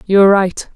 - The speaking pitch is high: Yes, high, 195 Hz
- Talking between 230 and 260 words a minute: Yes, fast, 235 wpm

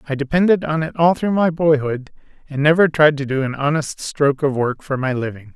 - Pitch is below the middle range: No, medium, 145 Hz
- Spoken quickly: Yes, fast, 225 wpm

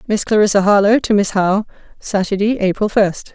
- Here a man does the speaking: No, female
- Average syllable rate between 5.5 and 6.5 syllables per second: Yes, 5.9 syllables/s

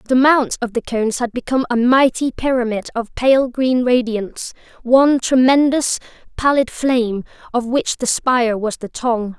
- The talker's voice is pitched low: No, high, 245 Hz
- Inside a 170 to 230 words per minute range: No, average, 155 wpm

